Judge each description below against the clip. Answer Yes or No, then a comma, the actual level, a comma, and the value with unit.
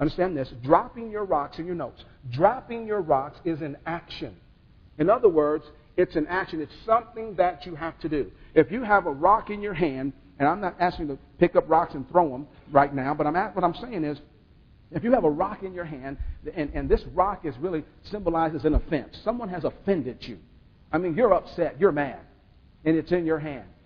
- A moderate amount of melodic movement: Yes, average, 4.6 semitones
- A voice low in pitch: No, medium, 165 Hz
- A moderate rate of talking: No, fast, 220 wpm